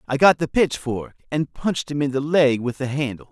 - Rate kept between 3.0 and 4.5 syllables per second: No, 5.4 syllables/s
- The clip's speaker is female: No, male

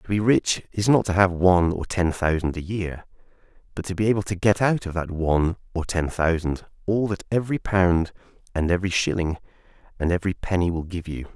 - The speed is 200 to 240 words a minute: Yes, fast, 205 wpm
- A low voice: Yes, very low, 90 Hz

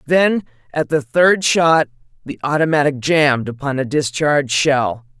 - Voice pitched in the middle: Yes, medium, 145 Hz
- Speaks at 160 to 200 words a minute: No, average, 140 wpm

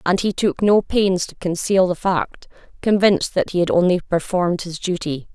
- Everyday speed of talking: Yes, average, 190 wpm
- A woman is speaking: Yes, female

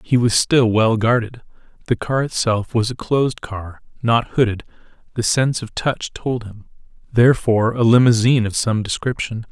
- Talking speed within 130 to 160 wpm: Yes, average, 150 wpm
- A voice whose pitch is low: Yes, low, 115 Hz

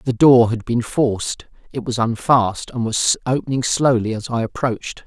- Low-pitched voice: Yes, low, 120 Hz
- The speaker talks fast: No, average, 180 wpm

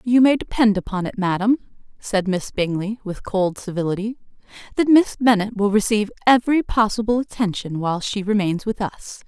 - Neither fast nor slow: Yes, average, 160 wpm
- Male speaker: No, female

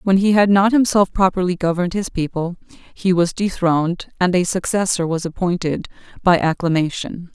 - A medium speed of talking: Yes, average, 155 wpm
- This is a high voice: No, medium, 180 Hz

